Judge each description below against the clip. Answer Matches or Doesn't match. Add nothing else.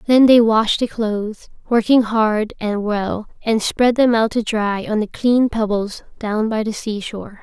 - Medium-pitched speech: Doesn't match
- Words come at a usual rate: Matches